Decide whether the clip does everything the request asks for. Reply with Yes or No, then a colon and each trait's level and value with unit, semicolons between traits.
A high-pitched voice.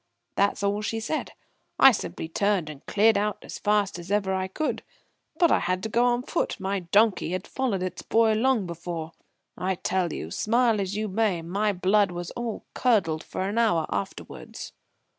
Yes: high, 200 Hz